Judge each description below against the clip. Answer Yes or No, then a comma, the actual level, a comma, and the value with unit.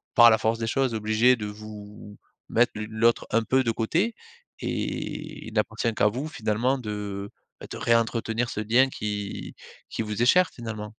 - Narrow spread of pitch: Yes, narrow, 2.2 semitones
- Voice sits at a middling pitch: No, low, 115 Hz